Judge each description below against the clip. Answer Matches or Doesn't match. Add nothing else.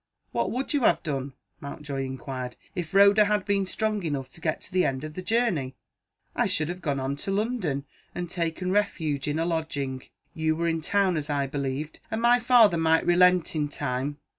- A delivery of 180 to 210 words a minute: Matches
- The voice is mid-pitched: Matches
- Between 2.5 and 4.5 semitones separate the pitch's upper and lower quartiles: Doesn't match